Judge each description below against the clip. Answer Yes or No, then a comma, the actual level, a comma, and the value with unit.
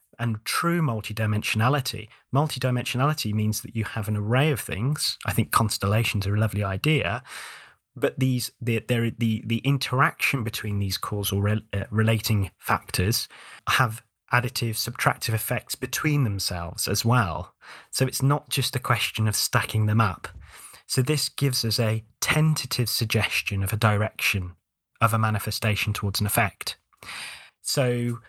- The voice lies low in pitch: Yes, low, 115 Hz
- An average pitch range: Yes, average, 3.1 semitones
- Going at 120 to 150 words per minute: Yes, average, 145 wpm